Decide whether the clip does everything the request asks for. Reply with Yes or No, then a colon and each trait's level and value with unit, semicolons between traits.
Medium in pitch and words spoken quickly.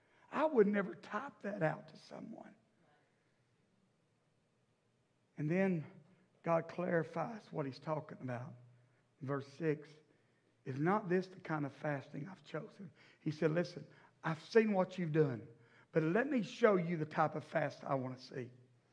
No: medium, 155 Hz; average, 155 wpm